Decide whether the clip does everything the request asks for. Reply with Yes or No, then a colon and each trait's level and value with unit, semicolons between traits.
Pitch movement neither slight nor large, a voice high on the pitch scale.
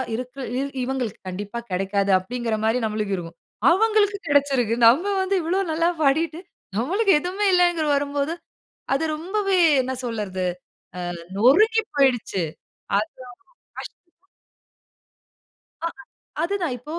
No: wide, 7.8 semitones; very high, 275 Hz